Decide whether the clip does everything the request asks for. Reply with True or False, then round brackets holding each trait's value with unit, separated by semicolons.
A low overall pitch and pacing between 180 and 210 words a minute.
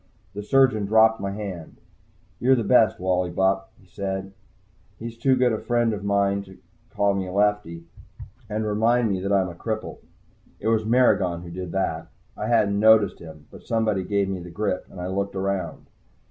True (100 Hz; 185 wpm)